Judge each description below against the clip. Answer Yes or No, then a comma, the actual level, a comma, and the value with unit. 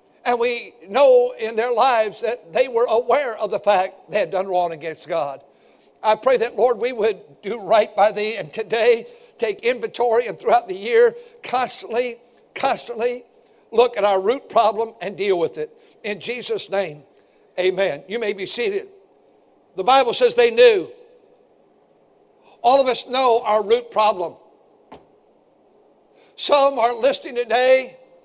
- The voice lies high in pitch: Yes, high, 245 Hz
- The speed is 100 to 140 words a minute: No, average, 155 wpm